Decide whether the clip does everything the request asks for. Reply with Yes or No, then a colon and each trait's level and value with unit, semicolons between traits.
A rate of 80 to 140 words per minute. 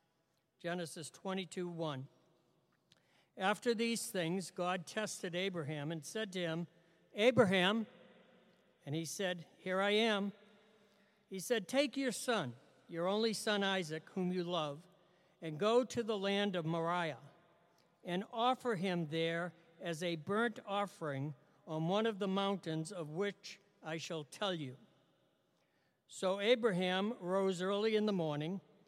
Yes: slow, 135 wpm